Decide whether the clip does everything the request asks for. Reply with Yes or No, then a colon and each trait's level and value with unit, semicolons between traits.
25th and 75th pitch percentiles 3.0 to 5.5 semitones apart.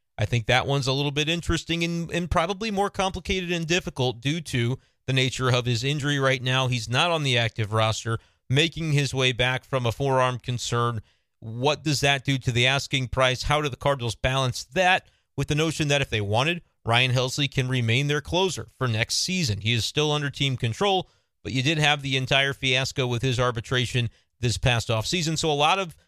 Yes: average, 3.6 semitones